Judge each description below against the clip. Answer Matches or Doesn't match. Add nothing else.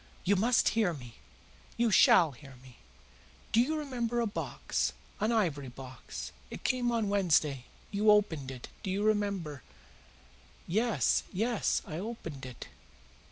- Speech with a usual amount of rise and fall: Doesn't match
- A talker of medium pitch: Doesn't match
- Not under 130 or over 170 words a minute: Matches